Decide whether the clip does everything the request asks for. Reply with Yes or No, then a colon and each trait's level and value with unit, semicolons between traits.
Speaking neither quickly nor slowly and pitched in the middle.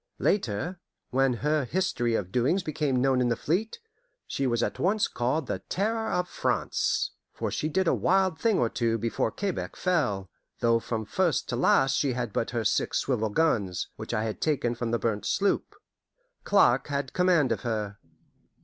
No: average, 180 wpm; low, 130 Hz